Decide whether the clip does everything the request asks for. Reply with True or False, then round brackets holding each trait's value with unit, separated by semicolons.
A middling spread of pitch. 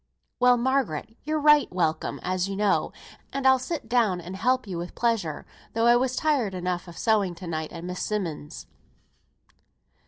False (5.9 semitones)